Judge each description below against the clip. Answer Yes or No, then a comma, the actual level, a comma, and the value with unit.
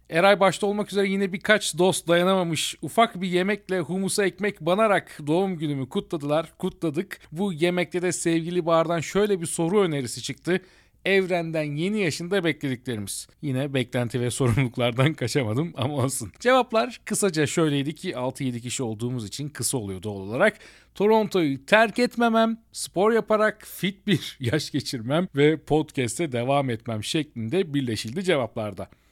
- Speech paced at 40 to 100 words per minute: No, fast, 140 wpm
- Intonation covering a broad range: Yes, wide, 6.3 semitones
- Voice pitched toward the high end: No, medium, 165 Hz